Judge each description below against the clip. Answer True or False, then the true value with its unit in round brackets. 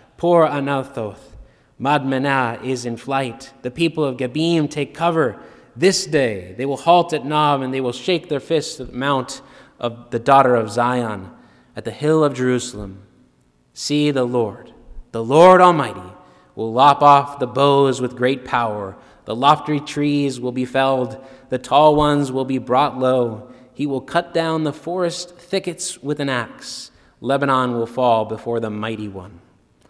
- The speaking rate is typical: True (165 wpm)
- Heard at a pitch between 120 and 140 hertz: True (135 Hz)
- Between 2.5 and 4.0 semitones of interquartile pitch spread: True (3.5 semitones)